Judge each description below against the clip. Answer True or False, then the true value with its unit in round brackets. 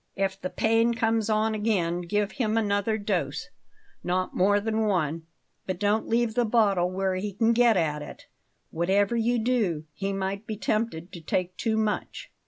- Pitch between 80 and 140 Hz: False (205 Hz)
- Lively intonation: False (3.3 semitones)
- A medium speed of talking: True (175 wpm)